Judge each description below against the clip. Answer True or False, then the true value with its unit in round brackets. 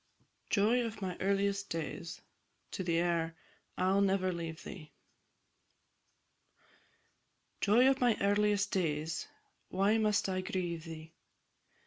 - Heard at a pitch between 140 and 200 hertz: True (190 Hz)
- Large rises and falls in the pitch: False (3.4 semitones)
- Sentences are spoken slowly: True (100 wpm)